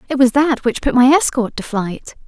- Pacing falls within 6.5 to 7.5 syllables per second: No, 5.0 syllables/s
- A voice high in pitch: Yes, very high, 250 Hz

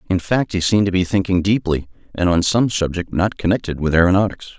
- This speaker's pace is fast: Yes, fast, 210 wpm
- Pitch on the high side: No, very low, 90 Hz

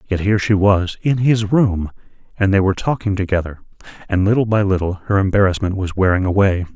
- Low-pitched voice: Yes, low, 100 Hz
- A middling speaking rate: Yes, average, 185 wpm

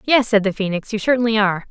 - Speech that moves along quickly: Yes, fast, 245 wpm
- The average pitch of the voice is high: Yes, high, 215 Hz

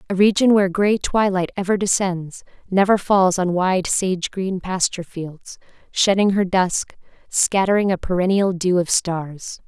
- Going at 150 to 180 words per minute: No, slow, 135 wpm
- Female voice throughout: Yes, female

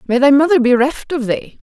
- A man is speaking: No, female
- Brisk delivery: Yes, fast, 250 wpm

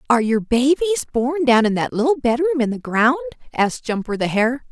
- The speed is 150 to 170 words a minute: No, fast, 205 wpm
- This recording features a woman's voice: Yes, female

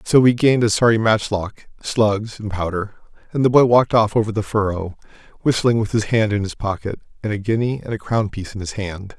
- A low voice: Yes, low, 105 Hz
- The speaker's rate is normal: No, fast, 220 wpm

